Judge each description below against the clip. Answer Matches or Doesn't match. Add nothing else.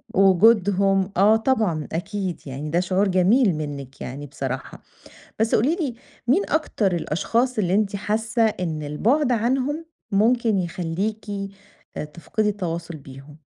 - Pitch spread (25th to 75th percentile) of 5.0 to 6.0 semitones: Matches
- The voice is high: Matches